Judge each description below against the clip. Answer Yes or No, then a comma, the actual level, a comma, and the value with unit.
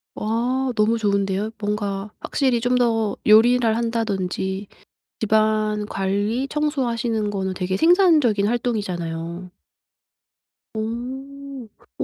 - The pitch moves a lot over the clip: No, average, 3.4 semitones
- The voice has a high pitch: Yes, high, 220 Hz